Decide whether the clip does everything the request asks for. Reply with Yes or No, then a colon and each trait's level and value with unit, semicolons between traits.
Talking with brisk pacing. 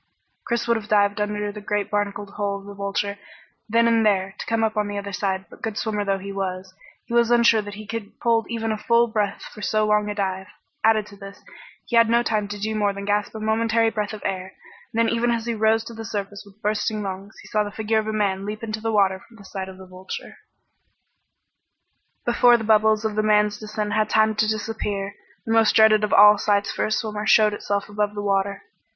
Yes: fast, 240 wpm